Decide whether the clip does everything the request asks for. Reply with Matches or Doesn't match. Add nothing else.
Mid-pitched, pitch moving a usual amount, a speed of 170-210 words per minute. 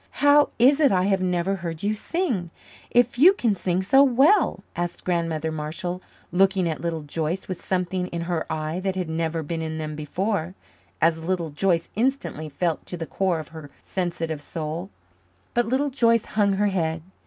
Matches